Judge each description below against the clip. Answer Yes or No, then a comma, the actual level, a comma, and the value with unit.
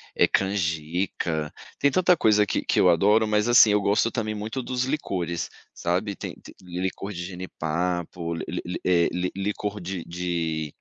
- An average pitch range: Yes, average, 3.4 semitones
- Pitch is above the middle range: No, very low, 95 Hz